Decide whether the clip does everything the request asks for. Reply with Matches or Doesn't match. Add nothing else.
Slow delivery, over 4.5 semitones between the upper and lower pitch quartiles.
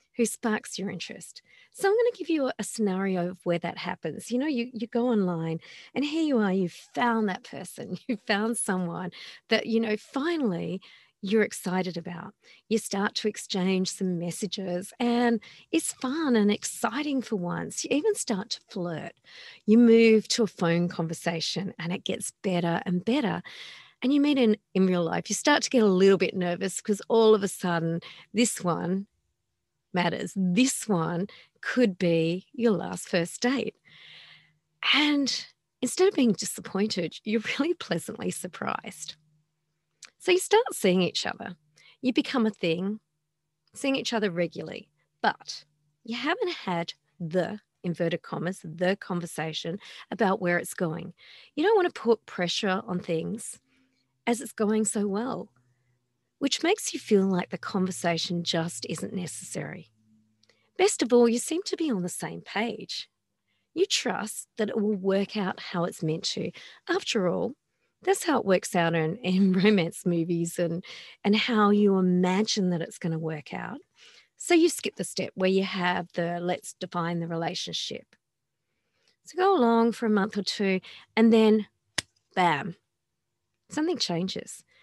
Doesn't match